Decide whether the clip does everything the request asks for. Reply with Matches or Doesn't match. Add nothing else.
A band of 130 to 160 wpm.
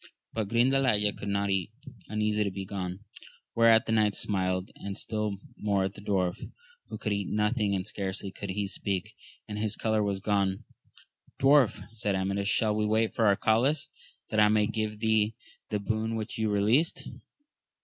Doesn't match